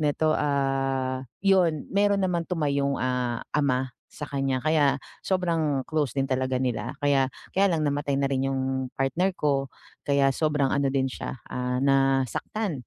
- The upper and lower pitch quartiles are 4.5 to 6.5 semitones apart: No, average, 2.8 semitones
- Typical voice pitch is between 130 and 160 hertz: Yes, medium, 140 Hz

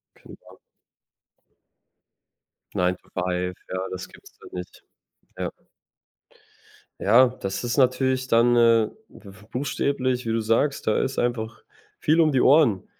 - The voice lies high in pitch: No, low, 120 Hz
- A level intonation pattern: No, average, 4.3 semitones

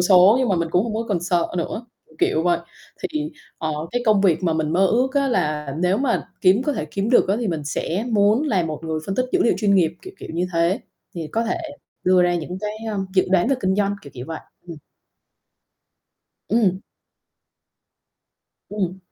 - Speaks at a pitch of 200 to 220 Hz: No, medium, 185 Hz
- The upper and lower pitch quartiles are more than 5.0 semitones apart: No, average, 4.3 semitones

